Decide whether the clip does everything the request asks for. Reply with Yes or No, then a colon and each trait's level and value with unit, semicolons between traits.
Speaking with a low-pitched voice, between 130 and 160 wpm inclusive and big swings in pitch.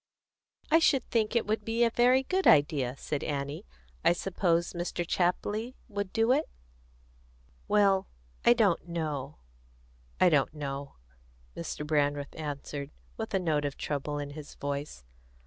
No: medium, 170 Hz; average, 145 wpm; wide, 7.0 semitones